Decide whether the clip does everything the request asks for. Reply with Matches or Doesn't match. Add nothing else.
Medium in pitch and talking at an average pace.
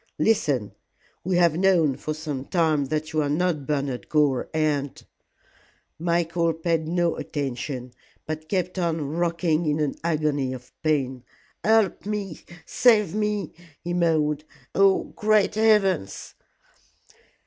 Doesn't match